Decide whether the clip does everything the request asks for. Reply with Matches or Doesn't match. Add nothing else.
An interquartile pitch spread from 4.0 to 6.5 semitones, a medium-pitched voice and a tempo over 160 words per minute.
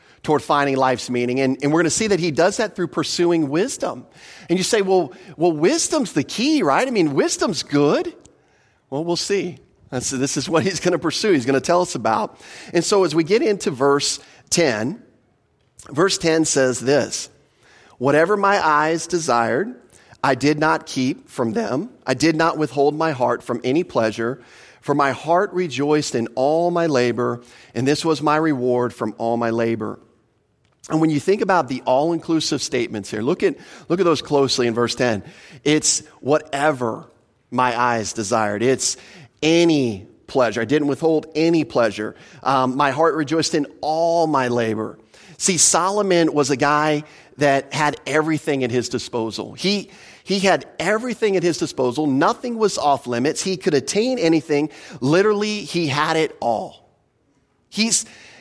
Matches